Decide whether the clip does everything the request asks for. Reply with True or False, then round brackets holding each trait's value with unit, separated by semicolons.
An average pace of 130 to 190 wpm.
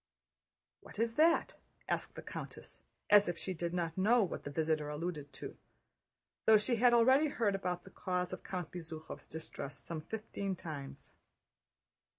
True (160 wpm)